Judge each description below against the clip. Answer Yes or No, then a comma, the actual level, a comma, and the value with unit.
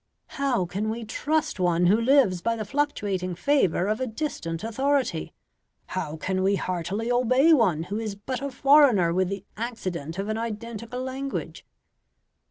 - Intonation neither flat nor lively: No, wide, 5.8 semitones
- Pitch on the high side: Yes, high, 220 Hz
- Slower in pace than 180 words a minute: Yes, average, 160 wpm